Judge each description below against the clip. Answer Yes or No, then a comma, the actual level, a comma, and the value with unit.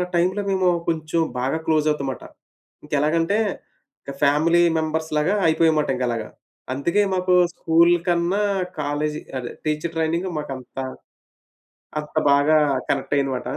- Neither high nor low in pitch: Yes, medium, 155 Hz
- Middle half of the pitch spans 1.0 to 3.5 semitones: Yes, average, 2.8 semitones